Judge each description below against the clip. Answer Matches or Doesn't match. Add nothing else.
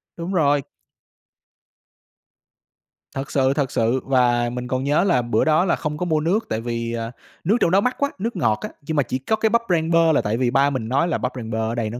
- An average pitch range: Doesn't match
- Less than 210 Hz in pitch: Matches